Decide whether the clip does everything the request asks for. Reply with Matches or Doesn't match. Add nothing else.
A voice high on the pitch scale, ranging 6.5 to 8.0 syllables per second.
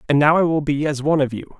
Doesn't match